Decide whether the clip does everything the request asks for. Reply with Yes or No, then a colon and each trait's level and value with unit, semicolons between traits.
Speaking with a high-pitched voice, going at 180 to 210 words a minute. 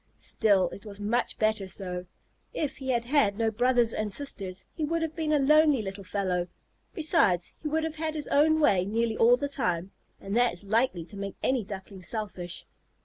Yes: high, 225 Hz; average, 200 wpm